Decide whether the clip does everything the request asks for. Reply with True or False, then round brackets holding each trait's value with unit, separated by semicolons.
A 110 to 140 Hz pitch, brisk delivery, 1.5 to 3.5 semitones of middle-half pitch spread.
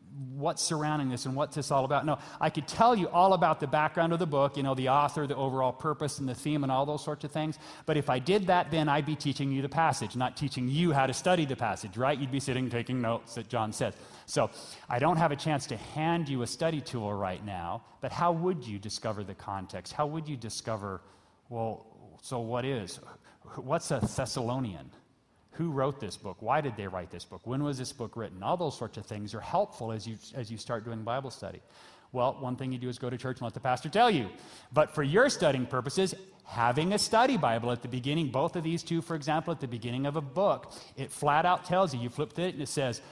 False (135 Hz; 245 wpm; 4.8 semitones)